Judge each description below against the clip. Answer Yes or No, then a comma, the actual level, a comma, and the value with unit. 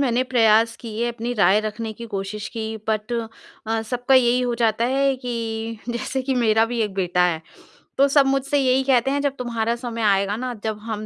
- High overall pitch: Yes, high, 230 Hz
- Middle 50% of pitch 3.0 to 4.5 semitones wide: No, narrow, 2.6 semitones